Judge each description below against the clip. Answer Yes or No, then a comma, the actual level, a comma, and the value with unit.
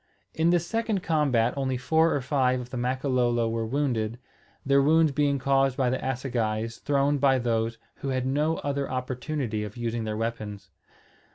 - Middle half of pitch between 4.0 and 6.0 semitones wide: No, average, 3.3 semitones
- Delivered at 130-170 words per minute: Yes, average, 165 wpm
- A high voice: No, low, 130 Hz